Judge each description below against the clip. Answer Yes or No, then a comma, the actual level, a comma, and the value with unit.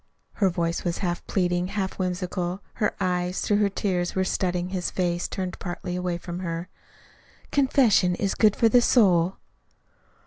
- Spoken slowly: No, average, 160 wpm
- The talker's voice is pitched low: No, medium, 180 Hz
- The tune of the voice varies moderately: No, narrow, 1.9 semitones